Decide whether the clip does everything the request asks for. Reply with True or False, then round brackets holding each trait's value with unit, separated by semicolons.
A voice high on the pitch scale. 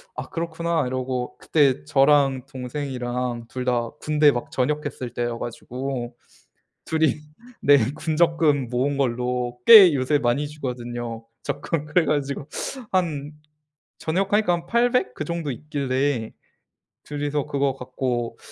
False (140 Hz)